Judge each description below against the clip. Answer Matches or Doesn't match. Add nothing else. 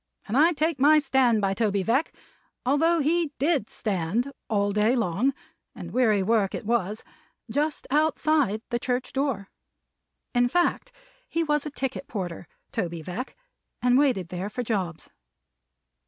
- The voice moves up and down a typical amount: Doesn't match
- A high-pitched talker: Matches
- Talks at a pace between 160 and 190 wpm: Doesn't match